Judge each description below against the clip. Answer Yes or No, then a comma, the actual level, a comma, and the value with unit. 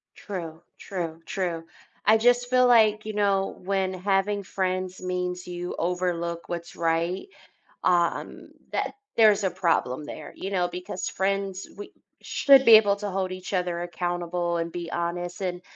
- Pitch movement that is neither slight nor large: No, narrow, 2.3 semitones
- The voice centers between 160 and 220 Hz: Yes, medium, 185 Hz